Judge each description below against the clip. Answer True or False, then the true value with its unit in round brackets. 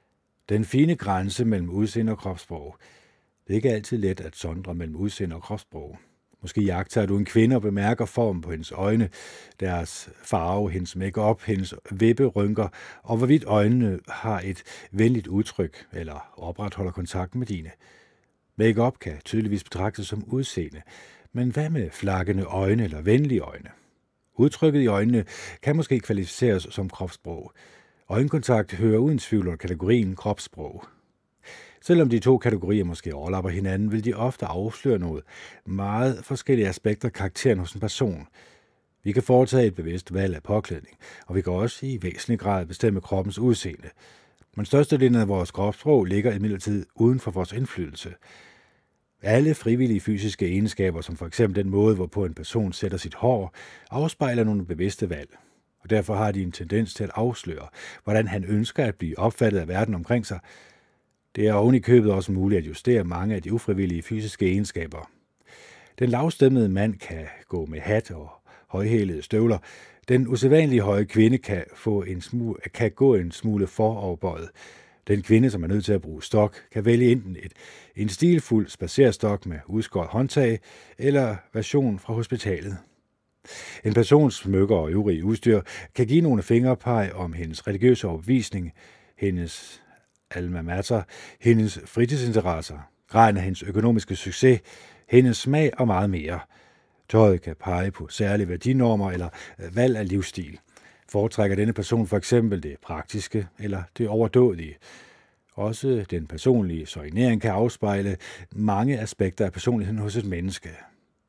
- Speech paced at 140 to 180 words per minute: True (155 wpm)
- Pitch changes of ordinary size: True (4.0 semitones)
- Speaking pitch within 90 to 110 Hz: True (105 Hz)